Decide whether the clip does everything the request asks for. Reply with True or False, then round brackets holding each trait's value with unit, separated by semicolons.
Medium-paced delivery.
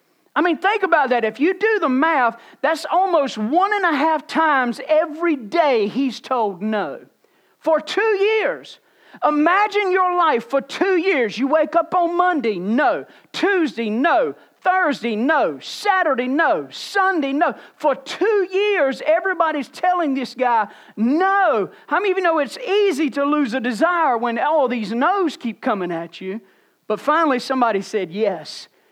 True (160 wpm)